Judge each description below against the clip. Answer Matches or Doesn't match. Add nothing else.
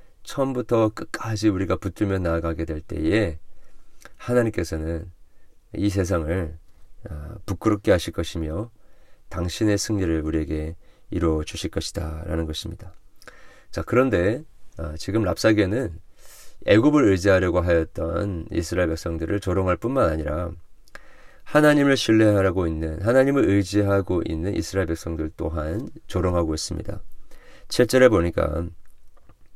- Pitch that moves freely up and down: Doesn't match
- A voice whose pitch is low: Matches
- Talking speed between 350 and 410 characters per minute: Doesn't match